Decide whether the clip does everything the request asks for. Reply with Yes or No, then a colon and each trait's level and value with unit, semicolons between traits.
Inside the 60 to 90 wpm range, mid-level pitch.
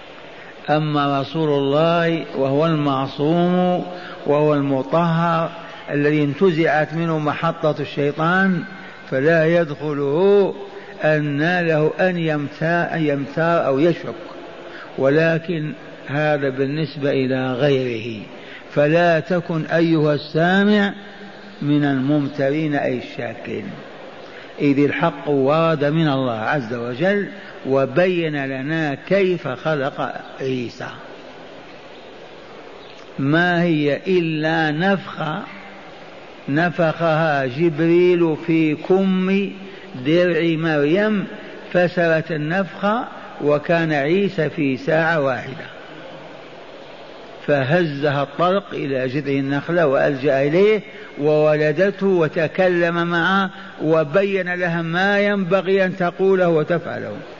Yes: average, 85 wpm; medium, 160 Hz